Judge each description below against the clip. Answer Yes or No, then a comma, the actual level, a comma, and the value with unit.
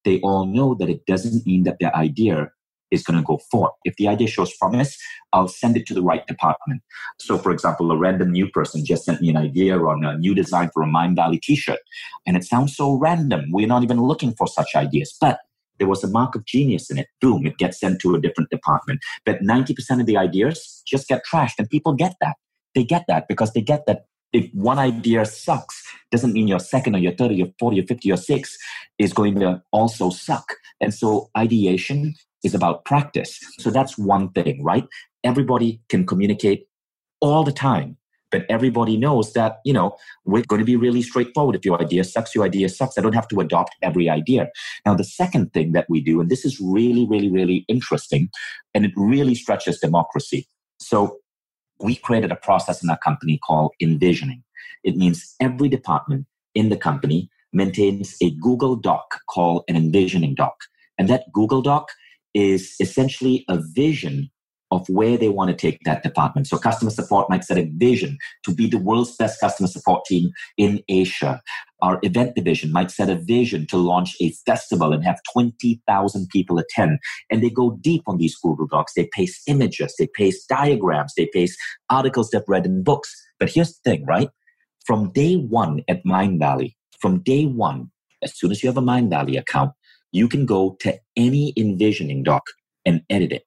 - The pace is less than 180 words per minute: No, average, 200 wpm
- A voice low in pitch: Yes, low, 110 Hz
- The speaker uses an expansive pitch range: Yes, wide, 6.1 semitones